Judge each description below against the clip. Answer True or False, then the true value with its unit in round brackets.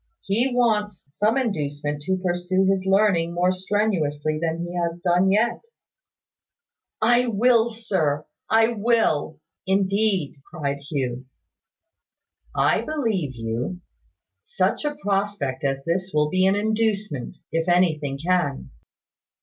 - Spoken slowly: True (125 wpm)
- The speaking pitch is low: False (185 Hz)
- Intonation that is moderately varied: False (5.8 semitones)